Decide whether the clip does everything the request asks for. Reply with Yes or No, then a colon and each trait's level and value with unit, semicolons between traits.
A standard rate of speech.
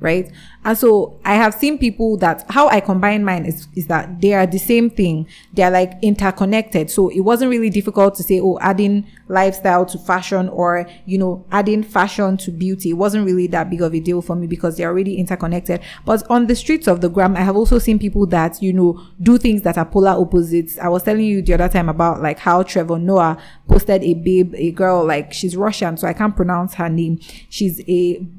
No: fast, 225 wpm